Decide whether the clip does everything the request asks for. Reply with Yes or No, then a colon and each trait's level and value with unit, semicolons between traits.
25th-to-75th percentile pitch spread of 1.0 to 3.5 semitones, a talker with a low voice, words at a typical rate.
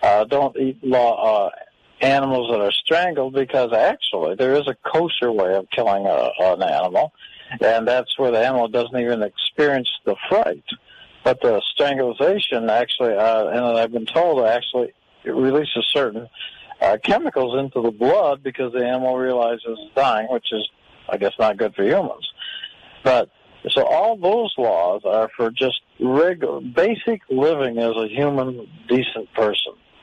Yes: average, 2.9 semitones; low, 125 Hz; average, 160 wpm